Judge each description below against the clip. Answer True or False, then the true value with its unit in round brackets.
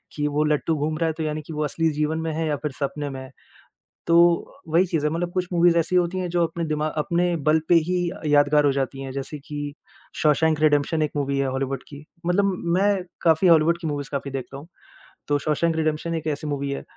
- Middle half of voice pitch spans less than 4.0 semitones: True (2.6 semitones)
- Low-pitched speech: False (155 Hz)